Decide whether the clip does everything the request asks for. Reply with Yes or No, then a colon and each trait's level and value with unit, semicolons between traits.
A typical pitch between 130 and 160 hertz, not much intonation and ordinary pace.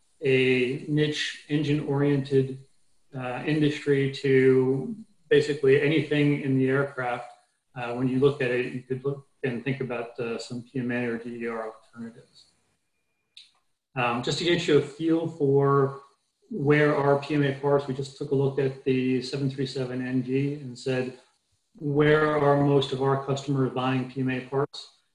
Yes: low, 135 Hz; narrow, 2.0 semitones; average, 145 wpm